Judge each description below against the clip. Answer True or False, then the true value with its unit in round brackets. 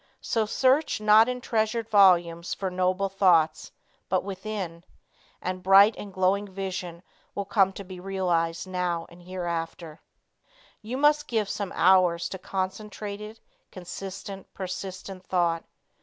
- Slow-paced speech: True (125 wpm)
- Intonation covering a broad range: False (2.5 semitones)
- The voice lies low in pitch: False (190 Hz)